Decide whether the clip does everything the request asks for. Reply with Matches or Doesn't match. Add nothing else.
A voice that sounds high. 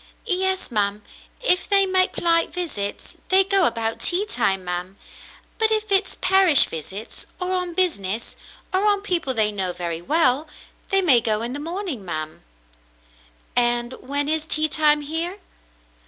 Matches